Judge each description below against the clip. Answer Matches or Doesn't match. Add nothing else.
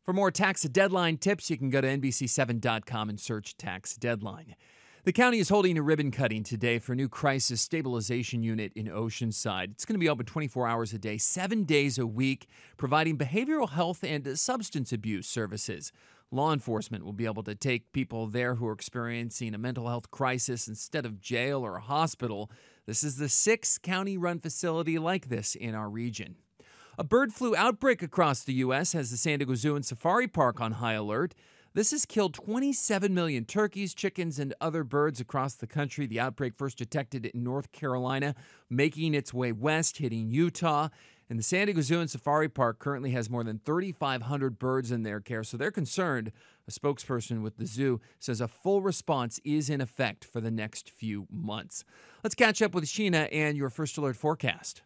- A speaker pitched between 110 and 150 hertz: Matches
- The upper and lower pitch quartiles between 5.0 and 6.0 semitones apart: Matches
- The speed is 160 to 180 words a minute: Doesn't match